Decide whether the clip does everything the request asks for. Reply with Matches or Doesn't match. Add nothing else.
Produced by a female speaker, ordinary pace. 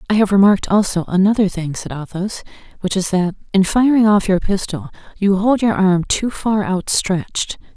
Matches